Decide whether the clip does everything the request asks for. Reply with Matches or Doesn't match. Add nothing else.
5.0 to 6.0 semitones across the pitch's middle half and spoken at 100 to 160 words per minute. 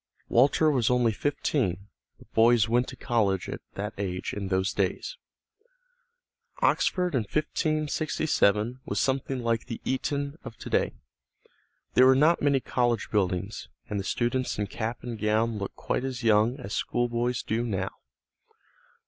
Doesn't match